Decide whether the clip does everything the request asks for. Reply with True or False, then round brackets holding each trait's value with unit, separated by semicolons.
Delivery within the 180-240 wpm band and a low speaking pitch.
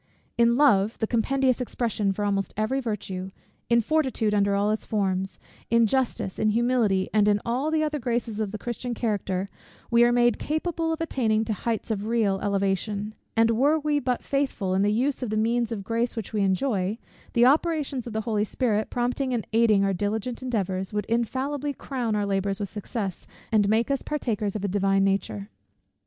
False (190 wpm; 220 Hz)